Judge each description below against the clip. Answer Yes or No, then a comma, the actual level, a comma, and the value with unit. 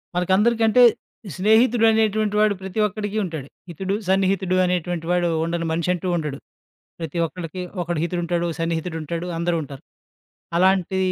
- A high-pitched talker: No, medium, 180 Hz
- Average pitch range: Yes, average, 3.0 semitones